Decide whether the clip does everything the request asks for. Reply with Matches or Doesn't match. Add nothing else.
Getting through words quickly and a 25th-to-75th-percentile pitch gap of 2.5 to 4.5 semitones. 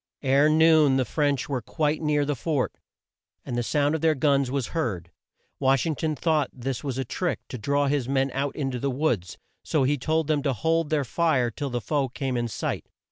Matches